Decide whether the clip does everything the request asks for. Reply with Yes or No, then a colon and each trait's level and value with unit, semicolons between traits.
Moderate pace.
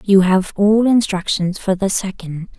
Yes: average, 165 wpm